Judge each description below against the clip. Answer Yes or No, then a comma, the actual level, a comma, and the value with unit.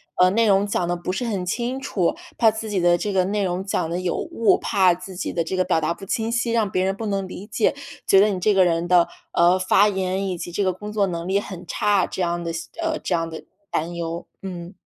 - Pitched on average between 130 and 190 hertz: Yes, medium, 185 Hz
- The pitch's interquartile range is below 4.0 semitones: Yes, average, 2.9 semitones